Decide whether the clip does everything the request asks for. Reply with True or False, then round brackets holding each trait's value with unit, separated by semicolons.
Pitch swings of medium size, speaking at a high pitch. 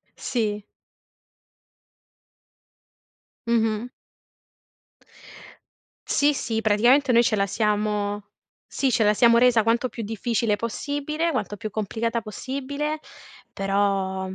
True (3.1 semitones; 225 Hz)